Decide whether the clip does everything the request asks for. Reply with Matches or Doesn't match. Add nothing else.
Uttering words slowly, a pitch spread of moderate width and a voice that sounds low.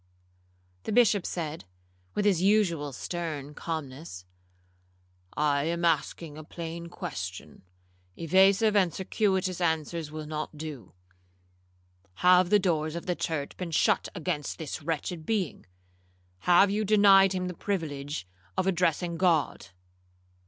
Doesn't match